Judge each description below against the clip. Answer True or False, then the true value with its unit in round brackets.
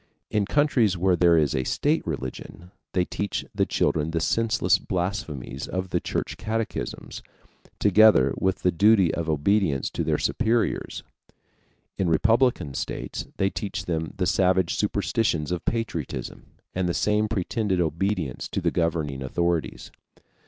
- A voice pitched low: True (90 Hz)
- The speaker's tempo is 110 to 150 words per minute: True (140 wpm)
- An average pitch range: True (4.5 semitones)